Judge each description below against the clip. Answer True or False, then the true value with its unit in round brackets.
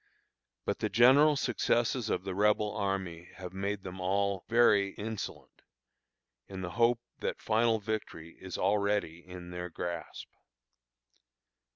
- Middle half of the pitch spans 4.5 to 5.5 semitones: False (3.3 semitones)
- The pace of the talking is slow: True (130 wpm)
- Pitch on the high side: False (100 Hz)